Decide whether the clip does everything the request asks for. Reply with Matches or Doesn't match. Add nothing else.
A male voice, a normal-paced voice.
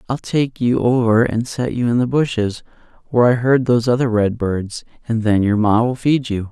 Doesn't match